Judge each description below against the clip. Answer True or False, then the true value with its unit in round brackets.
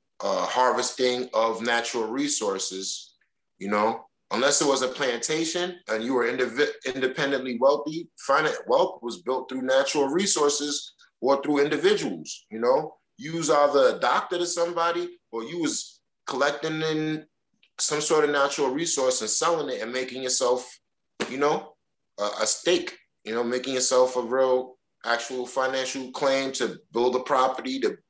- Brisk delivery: False (155 wpm)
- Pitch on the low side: True (130 Hz)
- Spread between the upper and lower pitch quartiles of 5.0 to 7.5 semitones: False (3.8 semitones)